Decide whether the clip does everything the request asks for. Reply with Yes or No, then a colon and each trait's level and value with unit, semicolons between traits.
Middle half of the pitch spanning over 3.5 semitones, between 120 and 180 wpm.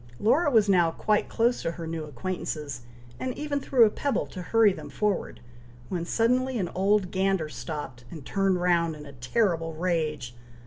Yes: average, 5.3 semitones; average, 175 wpm